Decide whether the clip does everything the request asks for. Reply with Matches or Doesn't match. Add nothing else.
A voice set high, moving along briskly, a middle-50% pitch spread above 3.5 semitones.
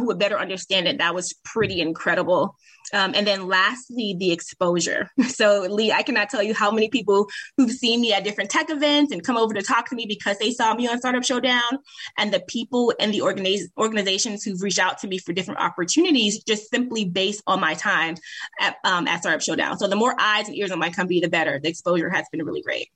Matches